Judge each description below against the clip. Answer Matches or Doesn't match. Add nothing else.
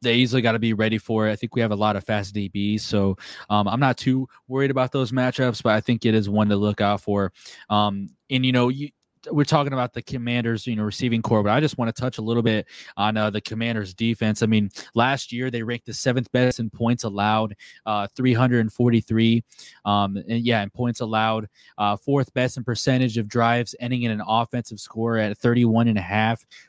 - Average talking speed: Doesn't match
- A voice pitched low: Matches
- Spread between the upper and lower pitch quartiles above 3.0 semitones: Doesn't match